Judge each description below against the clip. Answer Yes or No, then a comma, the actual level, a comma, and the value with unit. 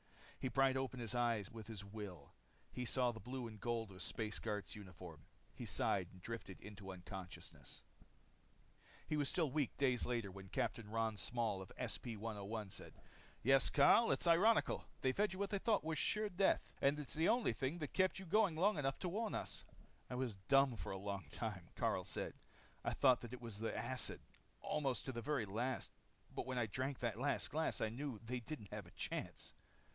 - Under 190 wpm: No, average, 200 wpm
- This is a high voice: No, low, 120 Hz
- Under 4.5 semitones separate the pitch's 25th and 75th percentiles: No, average, 5.2 semitones